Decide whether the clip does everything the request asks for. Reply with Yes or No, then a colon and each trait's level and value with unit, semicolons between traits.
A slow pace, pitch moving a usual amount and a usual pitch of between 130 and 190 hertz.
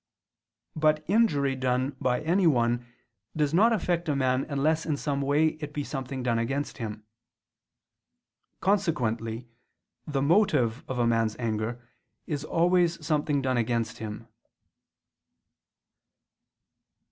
Yes: slow, 115 wpm; average, 4.5 semitones; medium, 140 Hz